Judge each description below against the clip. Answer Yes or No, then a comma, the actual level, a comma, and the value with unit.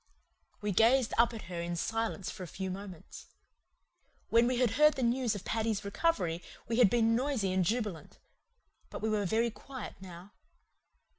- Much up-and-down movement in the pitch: No, average, 4.0 semitones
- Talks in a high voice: Yes, high, 220 Hz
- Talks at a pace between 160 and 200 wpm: Yes, average, 170 wpm